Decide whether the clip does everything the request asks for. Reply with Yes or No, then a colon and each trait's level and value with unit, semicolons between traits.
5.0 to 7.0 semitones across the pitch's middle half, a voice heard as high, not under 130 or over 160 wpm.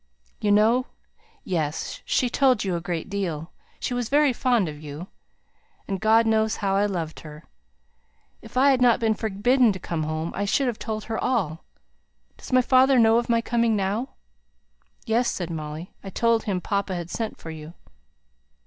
No: average, 5.3 semitones; high, 210 Hz; average, 180 wpm